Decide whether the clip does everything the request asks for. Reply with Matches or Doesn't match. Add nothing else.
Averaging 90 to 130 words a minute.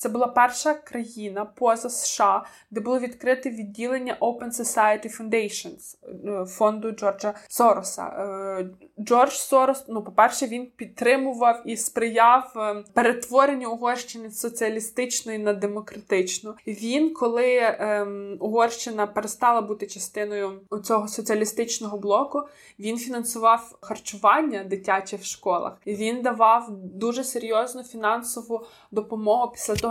Matches